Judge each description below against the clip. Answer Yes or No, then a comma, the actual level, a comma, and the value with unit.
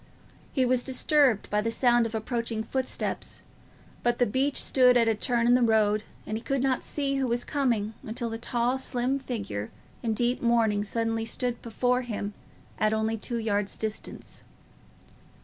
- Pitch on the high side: Yes, high, 235 Hz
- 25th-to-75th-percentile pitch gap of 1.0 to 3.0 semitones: Yes, narrow, 2.4 semitones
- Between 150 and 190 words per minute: Yes, average, 170 wpm